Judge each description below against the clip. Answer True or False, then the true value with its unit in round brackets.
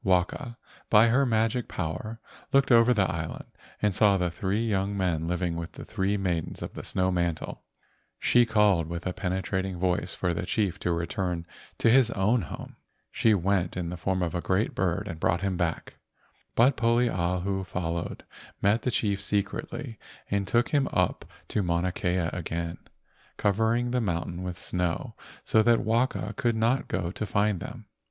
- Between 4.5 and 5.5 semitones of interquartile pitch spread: False (4.1 semitones)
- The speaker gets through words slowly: False (175 wpm)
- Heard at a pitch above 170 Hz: False (95 Hz)